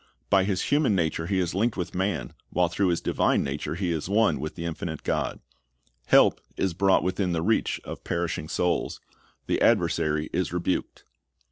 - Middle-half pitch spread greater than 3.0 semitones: No, average, 2.7 semitones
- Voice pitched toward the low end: Yes, very low, 90 Hz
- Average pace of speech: Yes, average, 175 wpm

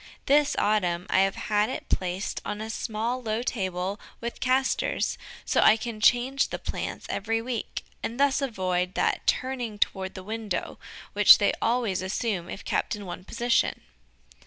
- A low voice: No, high, 215 Hz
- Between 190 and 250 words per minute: No, average, 160 wpm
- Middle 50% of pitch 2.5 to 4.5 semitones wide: Yes, average, 4.1 semitones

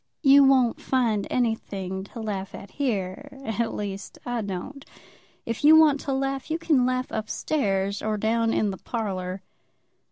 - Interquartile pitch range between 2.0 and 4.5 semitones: No, average, 5.2 semitones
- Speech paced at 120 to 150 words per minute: No, average, 160 wpm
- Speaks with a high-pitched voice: Yes, high, 230 Hz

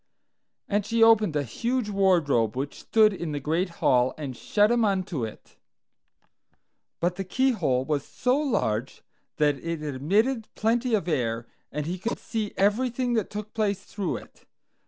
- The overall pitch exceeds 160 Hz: Yes, high, 190 Hz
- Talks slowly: No, average, 155 wpm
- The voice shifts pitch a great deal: Yes, wide, 7.2 semitones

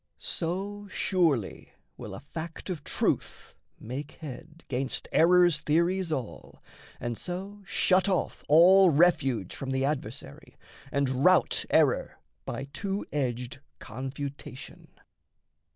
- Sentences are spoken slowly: Yes, slow, 110 wpm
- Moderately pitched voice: Yes, medium, 155 Hz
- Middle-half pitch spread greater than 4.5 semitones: Yes, wide, 5.4 semitones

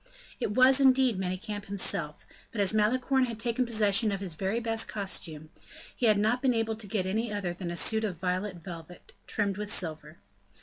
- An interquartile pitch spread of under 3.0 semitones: No, average, 3.5 semitones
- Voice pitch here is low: No, high, 205 Hz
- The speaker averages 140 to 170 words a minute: No, average, 190 wpm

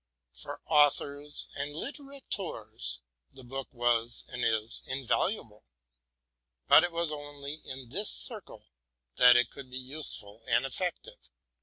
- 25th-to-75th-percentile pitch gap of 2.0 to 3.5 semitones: No, average, 4.2 semitones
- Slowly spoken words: Yes, slow, 130 wpm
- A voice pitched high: No, medium, 140 Hz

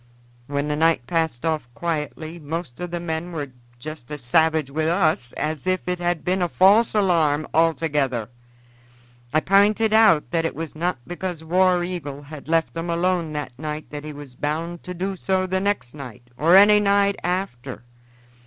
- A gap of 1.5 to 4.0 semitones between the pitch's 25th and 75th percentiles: Yes, average, 3.4 semitones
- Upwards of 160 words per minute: Yes, average, 180 wpm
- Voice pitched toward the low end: No, medium, 165 Hz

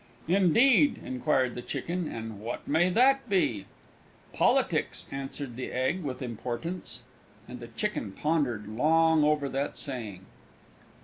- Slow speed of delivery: Yes, slow, 125 wpm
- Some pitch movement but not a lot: No, wide, 6.1 semitones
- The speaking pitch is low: No, medium, 145 Hz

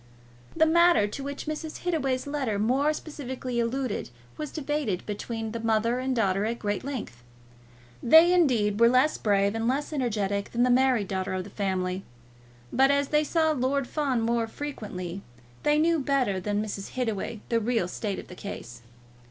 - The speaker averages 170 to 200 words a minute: Yes, average, 175 wpm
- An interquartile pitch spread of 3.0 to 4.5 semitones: No, wide, 5.4 semitones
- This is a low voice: No, high, 240 Hz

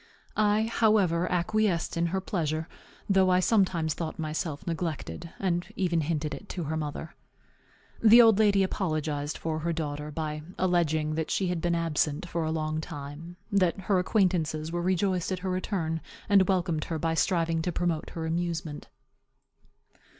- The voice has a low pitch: No, medium, 170 Hz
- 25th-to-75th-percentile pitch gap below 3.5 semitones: Yes, average, 2.9 semitones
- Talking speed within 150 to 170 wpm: Yes, average, 160 wpm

